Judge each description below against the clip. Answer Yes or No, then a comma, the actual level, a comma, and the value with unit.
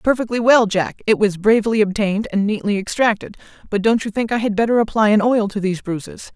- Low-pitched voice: No, high, 215 Hz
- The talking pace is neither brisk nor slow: No, fast, 215 wpm